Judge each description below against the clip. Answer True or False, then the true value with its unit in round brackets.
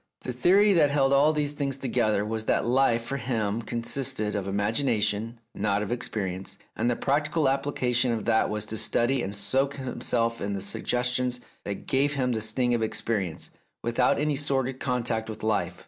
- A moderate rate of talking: True (180 wpm)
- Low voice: True (120 Hz)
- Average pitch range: True (3.9 semitones)